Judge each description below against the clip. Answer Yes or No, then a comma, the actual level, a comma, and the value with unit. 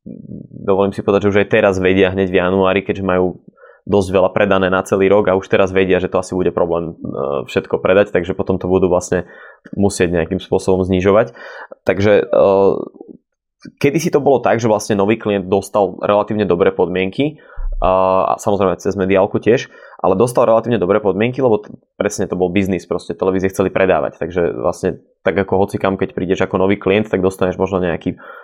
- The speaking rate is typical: No, fast, 180 wpm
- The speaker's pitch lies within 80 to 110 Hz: Yes, very low, 95 Hz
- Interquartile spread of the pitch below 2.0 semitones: Yes, narrow, 1.3 semitones